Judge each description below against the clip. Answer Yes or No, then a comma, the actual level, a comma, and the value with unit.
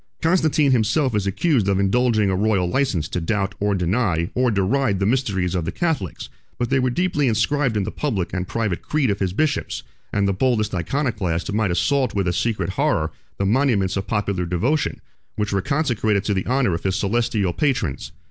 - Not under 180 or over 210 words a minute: Yes, average, 195 wpm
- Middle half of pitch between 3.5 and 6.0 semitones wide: Yes, wide, 5.5 semitones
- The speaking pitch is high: No, low, 105 Hz